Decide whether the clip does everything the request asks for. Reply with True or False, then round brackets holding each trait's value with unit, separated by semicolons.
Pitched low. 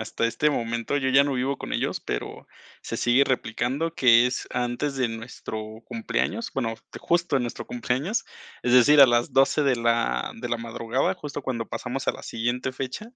True (125 Hz)